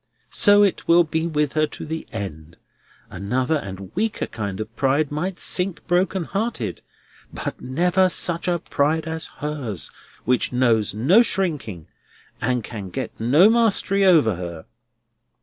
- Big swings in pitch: Yes, wide, 8.3 semitones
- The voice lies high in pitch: No, medium, 150 Hz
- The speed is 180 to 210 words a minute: No, average, 145 wpm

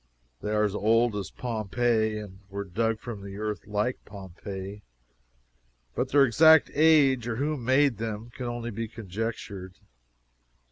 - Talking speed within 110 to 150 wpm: Yes, average, 140 wpm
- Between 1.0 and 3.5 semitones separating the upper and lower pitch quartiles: Yes, average, 2.9 semitones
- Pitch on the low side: Yes, low, 115 Hz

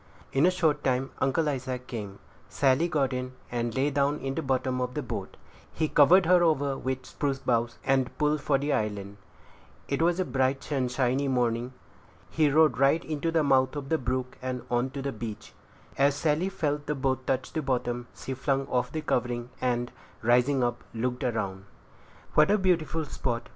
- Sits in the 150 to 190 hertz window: No, low, 135 Hz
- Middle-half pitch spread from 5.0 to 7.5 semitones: No, average, 3.0 semitones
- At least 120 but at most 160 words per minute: No, average, 190 wpm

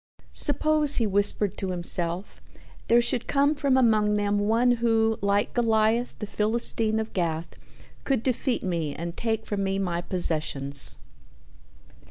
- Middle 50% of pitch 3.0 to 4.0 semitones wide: No, average, 4.4 semitones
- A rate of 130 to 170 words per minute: Yes, average, 140 wpm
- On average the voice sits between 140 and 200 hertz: No, high, 210 Hz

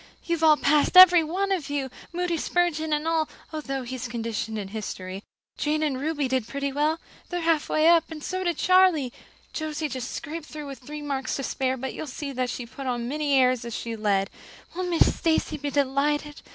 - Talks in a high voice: Yes, very high, 295 Hz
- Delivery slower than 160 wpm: No, fast, 205 wpm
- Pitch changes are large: No, average, 3.7 semitones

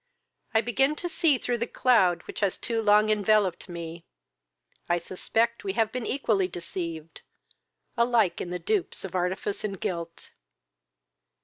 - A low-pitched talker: No, high, 205 Hz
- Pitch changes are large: No, average, 4.9 semitones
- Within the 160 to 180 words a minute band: No, average, 140 wpm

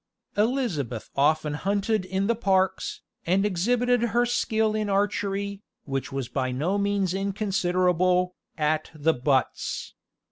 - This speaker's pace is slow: Yes, slow, 120 wpm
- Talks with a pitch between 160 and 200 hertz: Yes, high, 190 Hz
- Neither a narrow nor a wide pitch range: Yes, average, 4.7 semitones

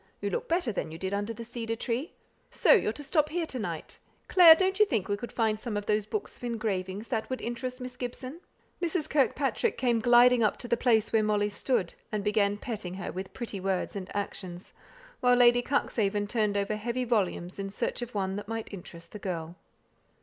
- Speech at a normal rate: No, fast, 210 wpm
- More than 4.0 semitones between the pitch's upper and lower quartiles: No, average, 3.7 semitones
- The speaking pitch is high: Yes, high, 225 Hz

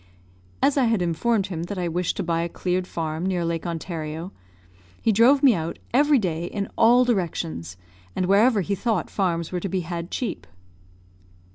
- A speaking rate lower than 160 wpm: No, average, 180 wpm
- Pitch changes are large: No, average, 4.6 semitones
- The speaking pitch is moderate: Yes, medium, 180 Hz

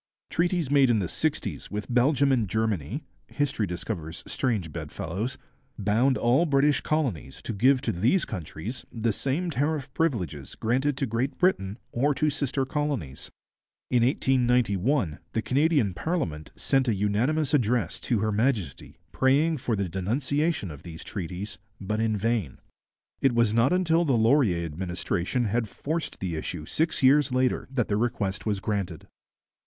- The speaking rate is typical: Yes, average, 150 wpm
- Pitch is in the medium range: No, low, 120 Hz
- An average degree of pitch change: No, wide, 5.9 semitones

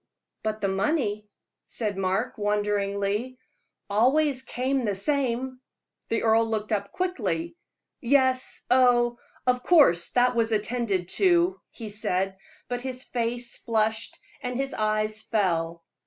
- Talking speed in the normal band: No, slow, 125 wpm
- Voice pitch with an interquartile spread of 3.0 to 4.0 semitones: Yes, average, 3.7 semitones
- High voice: Yes, high, 230 Hz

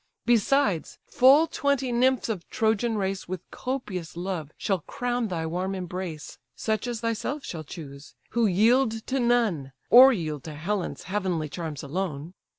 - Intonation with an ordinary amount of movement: No, wide, 6.3 semitones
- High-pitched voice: Yes, high, 195 Hz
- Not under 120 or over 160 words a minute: Yes, average, 150 wpm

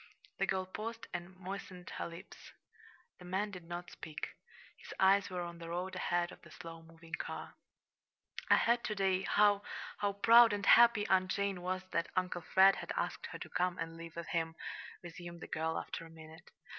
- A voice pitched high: No, medium, 180 Hz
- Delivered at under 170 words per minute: No, average, 195 wpm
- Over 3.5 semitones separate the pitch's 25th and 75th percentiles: No, narrow, 2.6 semitones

